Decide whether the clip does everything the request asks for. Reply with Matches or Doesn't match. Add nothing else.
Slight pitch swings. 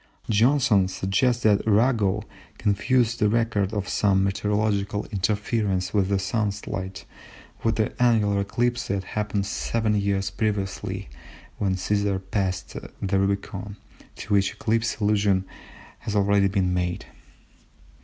Matches